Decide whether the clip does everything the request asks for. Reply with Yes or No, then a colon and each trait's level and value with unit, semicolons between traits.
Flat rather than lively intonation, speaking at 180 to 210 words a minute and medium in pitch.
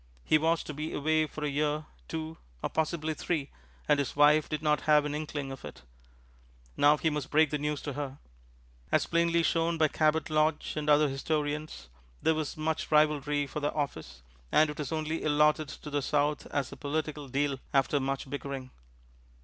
Yes: narrow, 1.4 semitones; average, 190 wpm; medium, 150 Hz